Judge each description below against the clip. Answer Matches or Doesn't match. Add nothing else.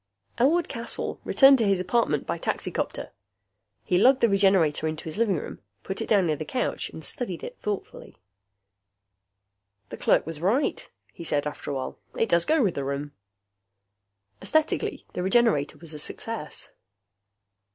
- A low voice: Doesn't match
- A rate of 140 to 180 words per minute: Matches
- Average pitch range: Doesn't match